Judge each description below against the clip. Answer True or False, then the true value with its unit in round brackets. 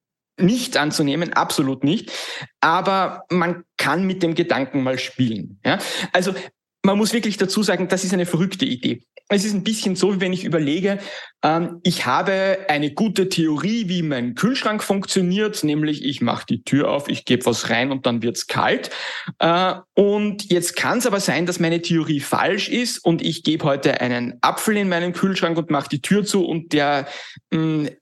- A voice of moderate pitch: True (175 Hz)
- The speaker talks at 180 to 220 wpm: True (185 wpm)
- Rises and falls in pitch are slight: False (4.6 semitones)